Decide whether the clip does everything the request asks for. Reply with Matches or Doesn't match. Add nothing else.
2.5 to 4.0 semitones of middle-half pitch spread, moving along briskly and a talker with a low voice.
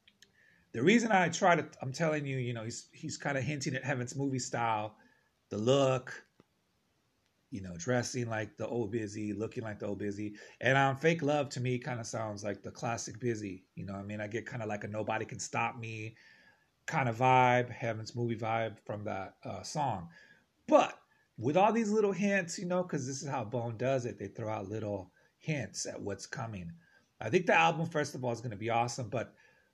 Doesn't match